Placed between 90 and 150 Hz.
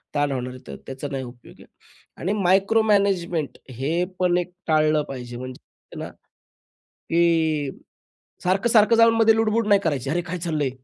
No: medium, 170 Hz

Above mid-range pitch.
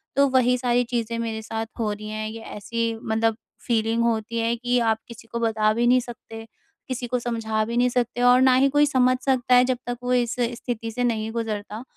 Yes: high, 235 Hz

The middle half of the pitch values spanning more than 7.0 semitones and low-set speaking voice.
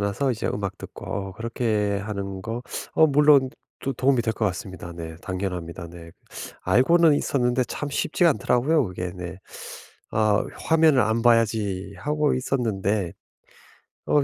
No: wide, 5.6 semitones; low, 110 Hz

